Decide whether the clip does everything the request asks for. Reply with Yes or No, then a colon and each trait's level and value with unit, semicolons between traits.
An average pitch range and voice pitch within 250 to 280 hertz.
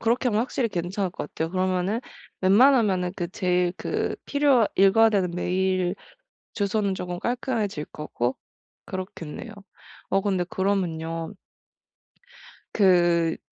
No: average, 3.0 semitones; high, 190 Hz